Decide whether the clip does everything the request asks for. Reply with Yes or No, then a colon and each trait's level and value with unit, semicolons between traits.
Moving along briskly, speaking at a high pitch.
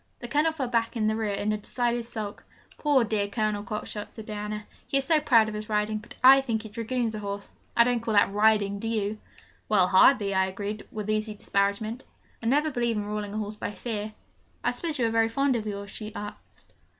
Yes: fast, 225 wpm; high, 215 Hz